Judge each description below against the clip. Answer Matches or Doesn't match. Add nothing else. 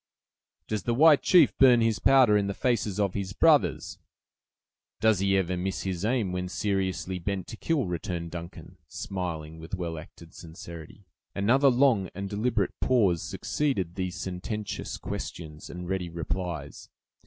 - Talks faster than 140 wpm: Matches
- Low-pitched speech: Matches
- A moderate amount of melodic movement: Matches